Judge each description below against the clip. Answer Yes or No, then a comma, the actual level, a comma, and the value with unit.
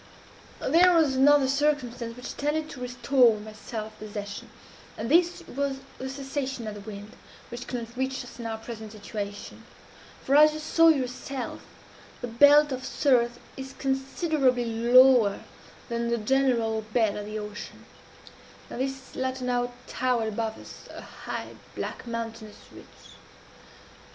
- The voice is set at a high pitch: Yes, very high, 250 Hz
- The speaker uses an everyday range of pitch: Yes, average, 3.2 semitones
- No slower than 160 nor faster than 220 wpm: No, average, 145 wpm